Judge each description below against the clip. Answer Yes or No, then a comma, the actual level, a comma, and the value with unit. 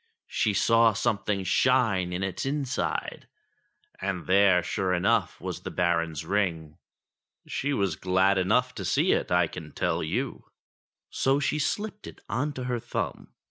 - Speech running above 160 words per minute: No, average, 155 wpm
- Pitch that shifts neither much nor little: No, wide, 5.9 semitones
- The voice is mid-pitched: No, low, 100 Hz